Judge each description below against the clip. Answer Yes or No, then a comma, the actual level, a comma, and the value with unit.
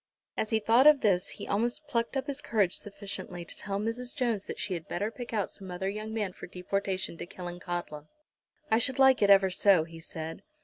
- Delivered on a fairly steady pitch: No, average, 4.2 semitones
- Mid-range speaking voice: No, high, 200 Hz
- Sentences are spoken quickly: Yes, fast, 215 wpm